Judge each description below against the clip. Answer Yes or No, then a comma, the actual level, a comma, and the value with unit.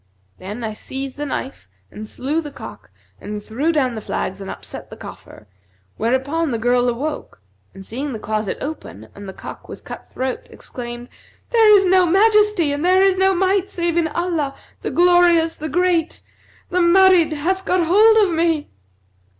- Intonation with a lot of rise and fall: Yes, wide, 6.7 semitones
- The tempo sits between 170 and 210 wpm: Yes, average, 175 wpm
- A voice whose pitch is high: Yes, very high, 315 Hz